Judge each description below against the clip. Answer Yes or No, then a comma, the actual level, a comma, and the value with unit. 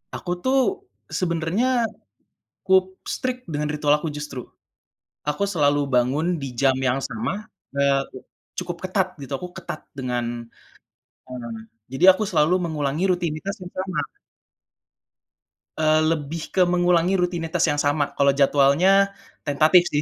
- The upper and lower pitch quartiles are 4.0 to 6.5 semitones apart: Yes, average, 4.5 semitones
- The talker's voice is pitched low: No, medium, 160 Hz